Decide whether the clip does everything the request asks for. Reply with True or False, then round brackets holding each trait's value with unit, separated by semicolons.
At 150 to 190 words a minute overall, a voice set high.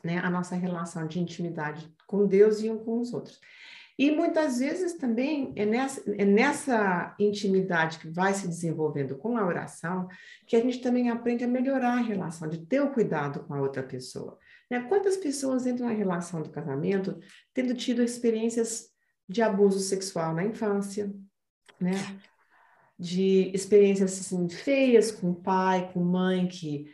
True (165 wpm; 200 Hz)